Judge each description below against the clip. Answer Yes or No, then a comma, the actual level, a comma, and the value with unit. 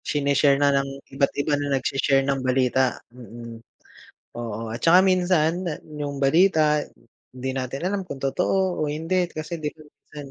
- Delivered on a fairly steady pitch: No, average, 3.5 semitones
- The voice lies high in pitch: No, medium, 145 Hz